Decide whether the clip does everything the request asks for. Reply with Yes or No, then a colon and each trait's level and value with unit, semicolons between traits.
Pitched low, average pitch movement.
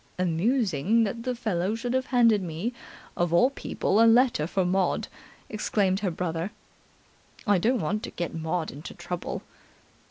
No: high, 195 Hz; average, 4.9 semitones